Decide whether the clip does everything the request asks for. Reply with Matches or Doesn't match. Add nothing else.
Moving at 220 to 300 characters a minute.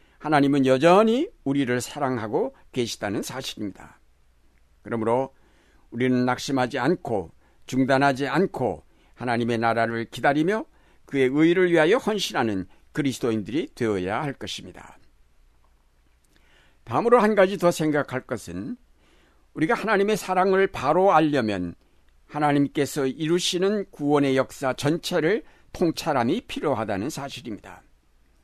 Matches